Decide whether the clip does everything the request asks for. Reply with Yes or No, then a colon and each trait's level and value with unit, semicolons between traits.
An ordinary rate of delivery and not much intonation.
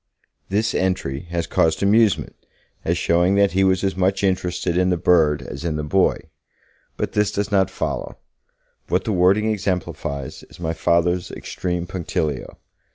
Yes: average, 160 wpm; narrow, 2.3 semitones